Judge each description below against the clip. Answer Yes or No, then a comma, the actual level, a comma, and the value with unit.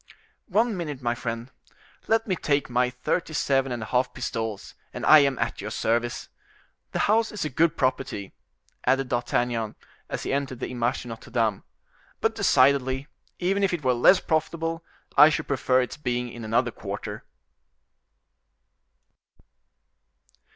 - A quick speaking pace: No, average, 150 wpm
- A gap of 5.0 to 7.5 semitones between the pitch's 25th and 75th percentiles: No, average, 4.3 semitones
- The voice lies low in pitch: Yes, low, 130 Hz